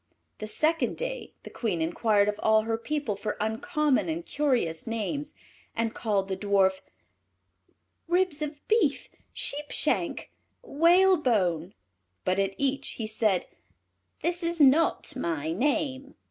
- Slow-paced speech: Yes, slow, 130 wpm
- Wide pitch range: Yes, wide, 7.0 semitones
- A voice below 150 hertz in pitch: No, high, 245 Hz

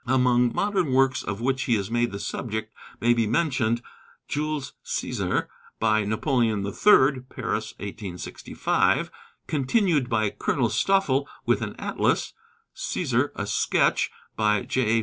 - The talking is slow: Yes, slow, 130 wpm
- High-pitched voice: No, low, 120 Hz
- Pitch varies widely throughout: No, average, 3.8 semitones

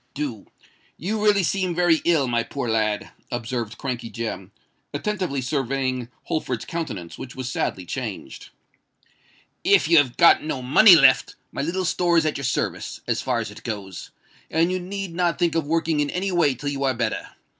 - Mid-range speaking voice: Yes, medium, 145 Hz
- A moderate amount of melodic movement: No, wide, 5.9 semitones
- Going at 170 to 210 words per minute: Yes, average, 180 wpm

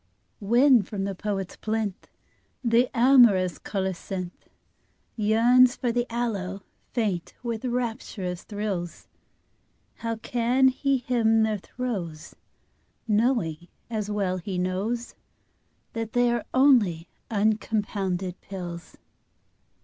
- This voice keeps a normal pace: No, slow, 100 wpm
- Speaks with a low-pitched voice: No, high, 215 Hz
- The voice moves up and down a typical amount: Yes, average, 4.1 semitones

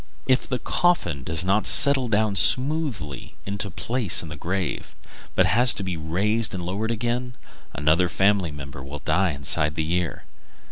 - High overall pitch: No, very low, 95 Hz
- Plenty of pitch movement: Yes, wide, 6.4 semitones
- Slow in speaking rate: No, average, 170 wpm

